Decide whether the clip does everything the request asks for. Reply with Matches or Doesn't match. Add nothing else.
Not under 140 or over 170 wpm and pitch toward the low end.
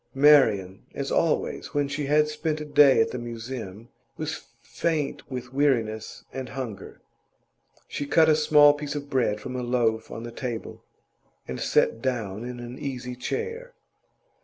Matches